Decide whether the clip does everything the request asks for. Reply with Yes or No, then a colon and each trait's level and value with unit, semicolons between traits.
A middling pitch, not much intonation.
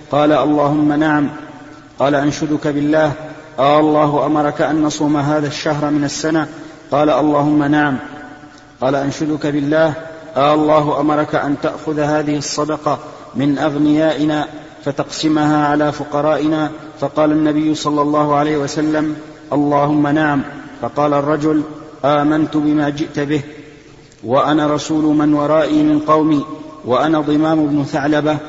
Yes: medium, 150 Hz; narrow, 0.7 semitones